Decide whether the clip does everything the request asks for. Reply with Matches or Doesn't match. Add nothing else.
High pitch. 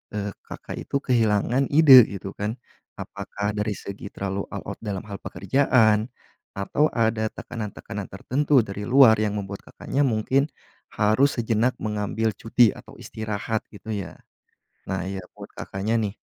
Doesn't match